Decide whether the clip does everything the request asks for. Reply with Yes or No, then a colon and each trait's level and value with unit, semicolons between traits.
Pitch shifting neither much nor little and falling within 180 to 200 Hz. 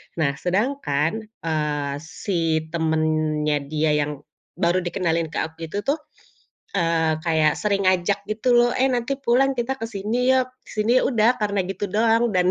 No: wide, 6.5 semitones; medium, 185 Hz